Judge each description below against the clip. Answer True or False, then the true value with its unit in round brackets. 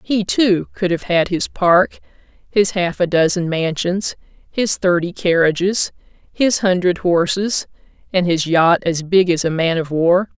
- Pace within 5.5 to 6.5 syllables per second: False (4.1 syllables/s)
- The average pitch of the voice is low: False (180 Hz)